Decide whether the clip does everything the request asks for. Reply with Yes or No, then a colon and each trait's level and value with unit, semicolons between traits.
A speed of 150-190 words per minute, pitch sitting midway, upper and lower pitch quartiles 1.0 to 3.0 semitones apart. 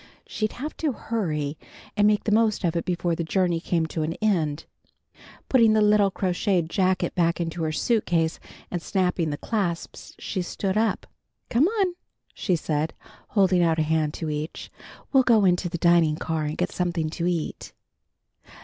No: average, 175 wpm; medium, 175 Hz; average, 4.3 semitones